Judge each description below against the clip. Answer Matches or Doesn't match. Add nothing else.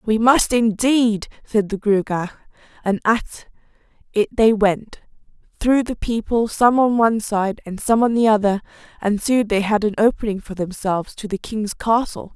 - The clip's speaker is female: Matches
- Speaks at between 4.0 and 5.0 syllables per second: Matches